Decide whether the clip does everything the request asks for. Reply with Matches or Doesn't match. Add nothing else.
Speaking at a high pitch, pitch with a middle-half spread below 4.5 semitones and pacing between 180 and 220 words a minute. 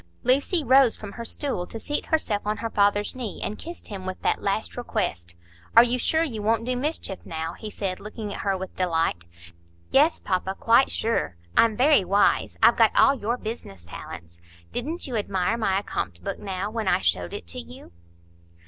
Doesn't match